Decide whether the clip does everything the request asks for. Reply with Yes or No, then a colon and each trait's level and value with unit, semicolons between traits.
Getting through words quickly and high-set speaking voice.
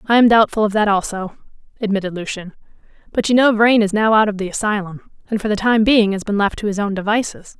Yes: fast, 235 wpm; high, 210 Hz